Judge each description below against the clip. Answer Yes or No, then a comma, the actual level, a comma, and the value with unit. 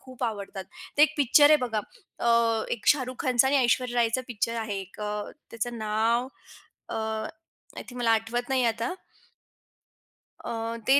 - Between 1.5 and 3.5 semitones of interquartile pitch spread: Yes, narrow, 2.6 semitones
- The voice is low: No, high, 235 Hz